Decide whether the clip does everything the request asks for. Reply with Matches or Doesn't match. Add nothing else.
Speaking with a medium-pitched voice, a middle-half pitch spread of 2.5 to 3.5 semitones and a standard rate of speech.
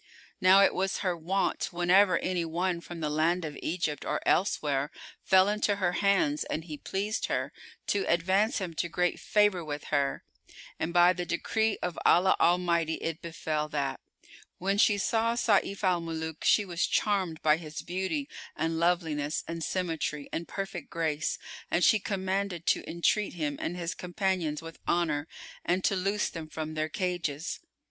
Matches